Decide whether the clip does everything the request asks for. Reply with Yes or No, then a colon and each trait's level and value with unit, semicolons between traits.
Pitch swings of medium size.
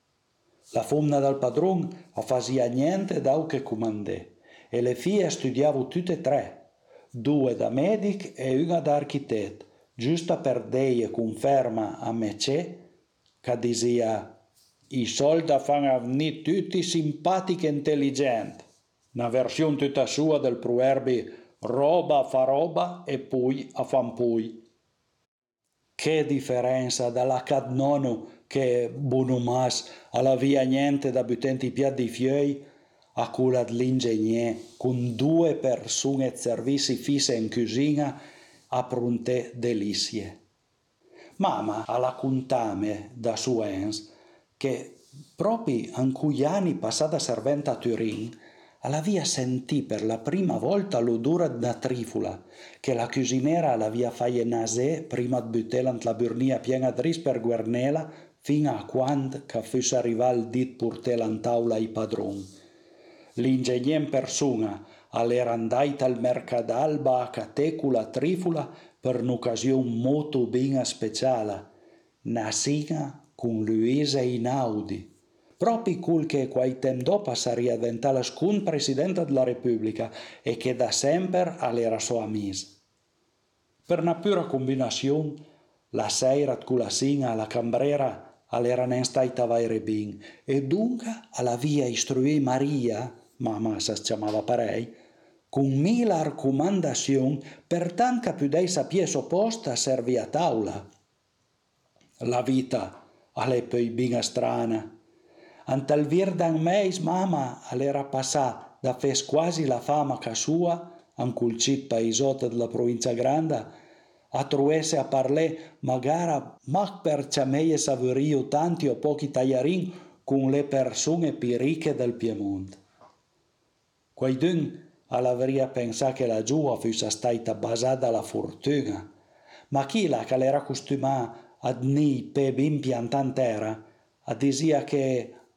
Yes: average, 3.6 semitones